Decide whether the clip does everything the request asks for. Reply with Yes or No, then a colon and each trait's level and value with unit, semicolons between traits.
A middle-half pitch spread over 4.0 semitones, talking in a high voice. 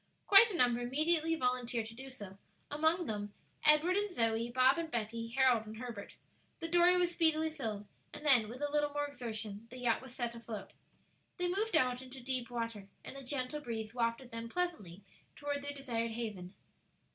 Yes: average, 4.8 semitones; very high, 255 Hz